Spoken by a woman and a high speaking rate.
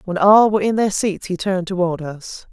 Yes: female; fast, 240 wpm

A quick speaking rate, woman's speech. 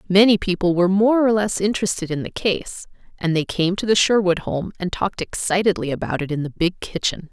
Yes: fast, 215 wpm; female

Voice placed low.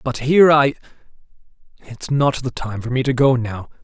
Yes: low, 130 Hz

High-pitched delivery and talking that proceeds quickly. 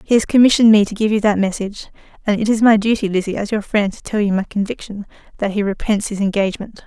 Yes: high, 205 Hz; fast, 235 wpm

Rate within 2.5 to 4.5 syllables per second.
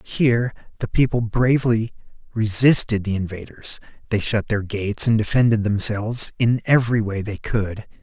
No: 5.1 syllables/s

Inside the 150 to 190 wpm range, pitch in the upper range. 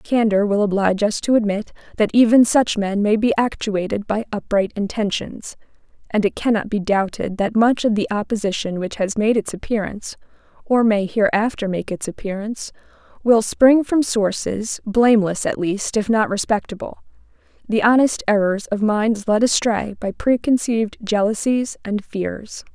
Yes: average, 155 wpm; high, 215 Hz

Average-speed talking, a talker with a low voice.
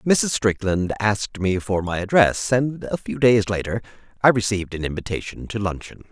Yes: average, 175 wpm; low, 105 Hz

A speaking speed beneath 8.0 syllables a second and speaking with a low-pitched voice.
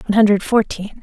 No: 6.9 syllables/s; high, 210 Hz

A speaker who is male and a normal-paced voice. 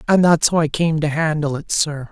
No: male; fast, 255 wpm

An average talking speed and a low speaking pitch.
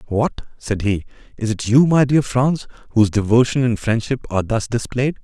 Yes: average, 185 wpm; low, 120 Hz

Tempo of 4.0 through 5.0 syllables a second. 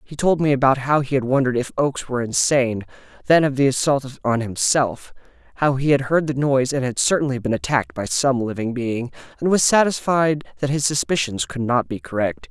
No: 5.8 syllables/s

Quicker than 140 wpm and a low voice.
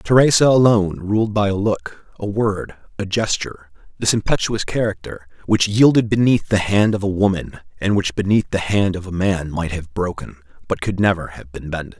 Yes: average, 190 wpm; low, 100 Hz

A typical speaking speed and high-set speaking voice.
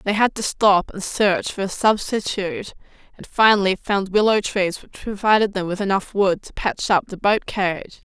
Yes: average, 195 wpm; high, 200 Hz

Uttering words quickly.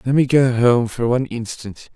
Yes: fast, 215 wpm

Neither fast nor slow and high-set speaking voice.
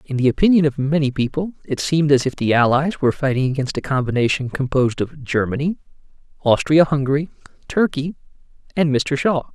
No: average, 165 wpm; medium, 140 Hz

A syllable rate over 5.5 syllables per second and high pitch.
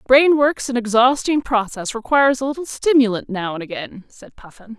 No: 5.2 syllables/s; high, 240 Hz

